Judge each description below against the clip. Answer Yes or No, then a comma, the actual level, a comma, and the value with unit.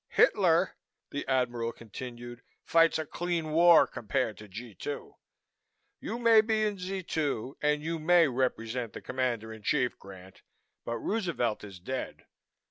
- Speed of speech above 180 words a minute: No, average, 145 wpm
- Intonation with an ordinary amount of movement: No, wide, 6.3 semitones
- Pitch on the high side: No, low, 130 Hz